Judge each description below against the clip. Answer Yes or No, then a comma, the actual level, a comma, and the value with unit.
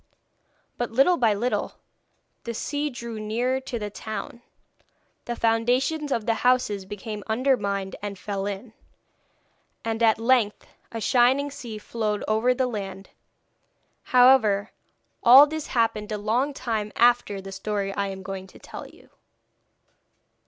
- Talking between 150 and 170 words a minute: No, average, 140 wpm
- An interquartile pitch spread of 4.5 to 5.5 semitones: No, average, 3.3 semitones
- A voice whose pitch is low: No, high, 225 Hz